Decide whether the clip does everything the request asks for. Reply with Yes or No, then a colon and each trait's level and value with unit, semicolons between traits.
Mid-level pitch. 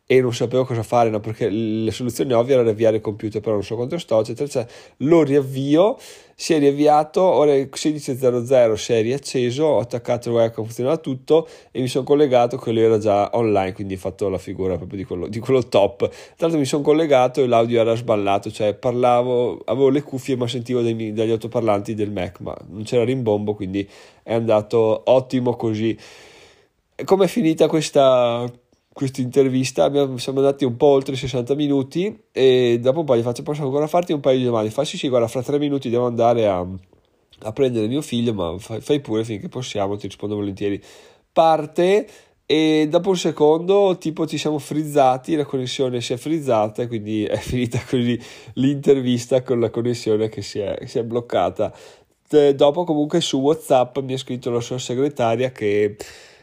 No: low, 125 Hz